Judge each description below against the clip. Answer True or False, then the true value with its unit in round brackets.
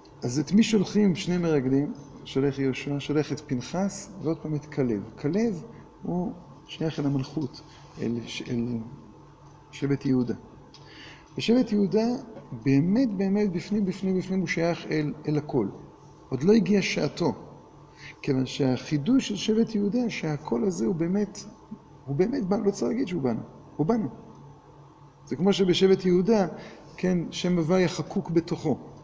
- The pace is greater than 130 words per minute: True (140 wpm)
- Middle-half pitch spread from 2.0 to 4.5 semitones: False (5.4 semitones)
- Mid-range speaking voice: True (160 Hz)